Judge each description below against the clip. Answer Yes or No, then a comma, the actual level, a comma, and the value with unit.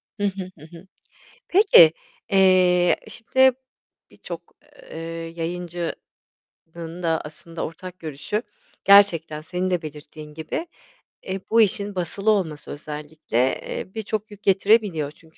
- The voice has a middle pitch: Yes, medium, 180 Hz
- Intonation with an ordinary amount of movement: Yes, average, 4.2 semitones